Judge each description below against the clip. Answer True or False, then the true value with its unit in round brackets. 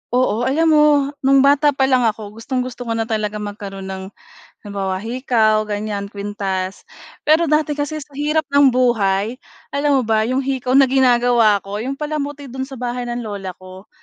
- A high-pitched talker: True (245 Hz)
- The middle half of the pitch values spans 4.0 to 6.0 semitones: True (4.7 semitones)